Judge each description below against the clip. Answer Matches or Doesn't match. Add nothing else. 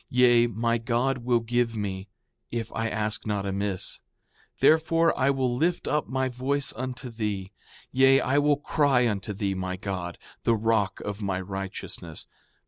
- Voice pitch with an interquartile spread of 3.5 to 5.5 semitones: Matches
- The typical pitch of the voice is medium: Doesn't match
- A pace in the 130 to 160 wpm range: Matches